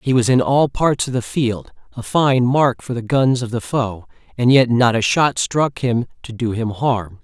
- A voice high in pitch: No, low, 125 Hz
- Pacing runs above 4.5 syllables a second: No, 4.3 syllables/s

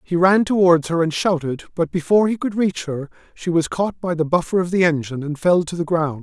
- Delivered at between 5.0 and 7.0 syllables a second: Yes, 5.7 syllables/s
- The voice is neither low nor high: Yes, medium, 170 Hz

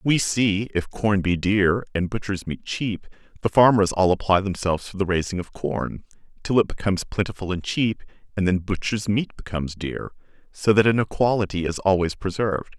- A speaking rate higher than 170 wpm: Yes, average, 185 wpm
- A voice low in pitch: Yes, low, 100 Hz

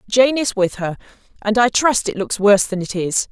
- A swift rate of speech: Yes, fast, 235 wpm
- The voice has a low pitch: No, high, 215 Hz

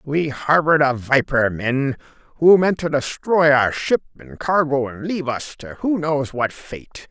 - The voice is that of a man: Yes, male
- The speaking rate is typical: Yes, average, 175 wpm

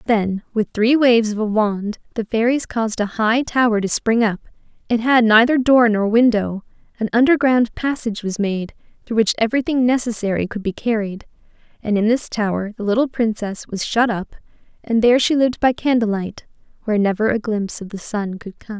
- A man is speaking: No, female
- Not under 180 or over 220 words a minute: Yes, average, 190 wpm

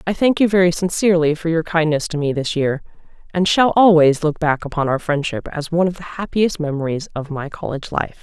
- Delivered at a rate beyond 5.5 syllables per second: Yes, 5.9 syllables/s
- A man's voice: No, female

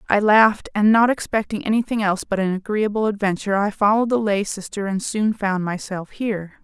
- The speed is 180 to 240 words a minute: Yes, average, 190 wpm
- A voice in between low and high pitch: No, high, 205 Hz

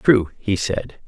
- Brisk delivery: No, average, 165 wpm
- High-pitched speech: No, low, 105 Hz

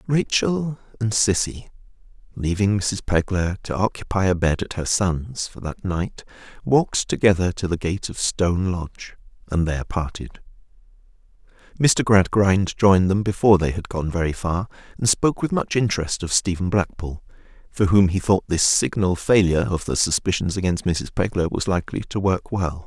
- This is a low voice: Yes, very low, 95 Hz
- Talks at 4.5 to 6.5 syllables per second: Yes, 5.0 syllables/s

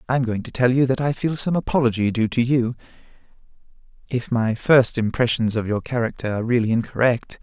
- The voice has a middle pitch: No, low, 120 Hz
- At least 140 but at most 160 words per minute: No, average, 195 wpm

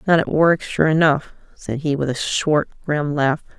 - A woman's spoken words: Yes, female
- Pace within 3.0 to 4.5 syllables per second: Yes, 4.4 syllables/s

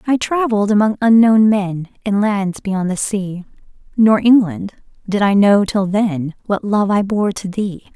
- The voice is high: Yes, high, 205 Hz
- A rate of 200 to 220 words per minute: No, average, 175 wpm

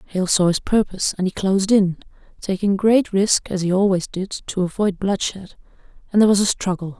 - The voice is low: No, high, 195 Hz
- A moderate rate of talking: Yes, average, 195 wpm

